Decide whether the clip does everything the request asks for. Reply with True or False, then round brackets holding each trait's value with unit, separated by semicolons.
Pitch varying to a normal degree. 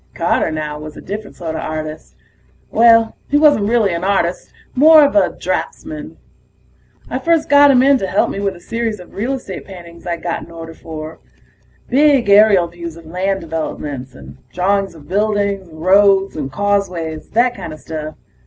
False (5.8 semitones)